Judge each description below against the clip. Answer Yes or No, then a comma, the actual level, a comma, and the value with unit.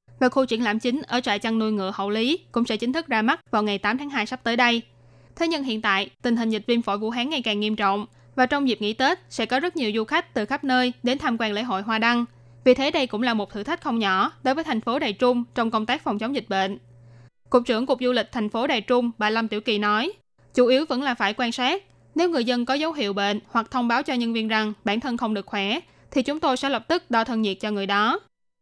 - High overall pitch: Yes, high, 235 Hz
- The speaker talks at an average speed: No, fast, 285 wpm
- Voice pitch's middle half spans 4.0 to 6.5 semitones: No, average, 3.5 semitones